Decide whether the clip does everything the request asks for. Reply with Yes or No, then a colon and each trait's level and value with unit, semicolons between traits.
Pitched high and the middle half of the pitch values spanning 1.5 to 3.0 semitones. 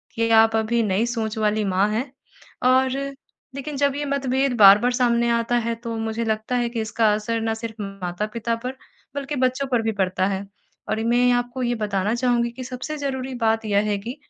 Yes: high, 230 Hz; average, 2.7 semitones